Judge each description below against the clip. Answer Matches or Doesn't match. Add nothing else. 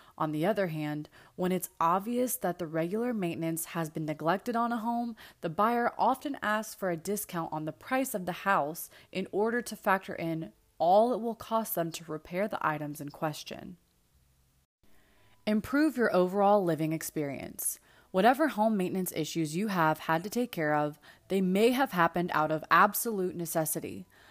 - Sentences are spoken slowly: Doesn't match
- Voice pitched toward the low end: Doesn't match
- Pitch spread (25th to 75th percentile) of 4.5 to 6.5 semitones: Matches